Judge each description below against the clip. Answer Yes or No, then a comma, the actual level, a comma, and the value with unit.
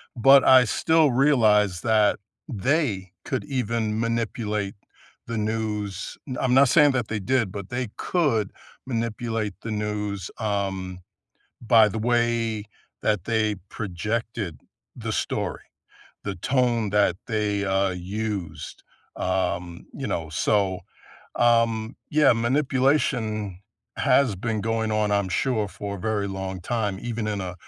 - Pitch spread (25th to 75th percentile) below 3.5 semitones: Yes, average, 2.9 semitones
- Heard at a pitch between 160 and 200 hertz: No, low, 110 Hz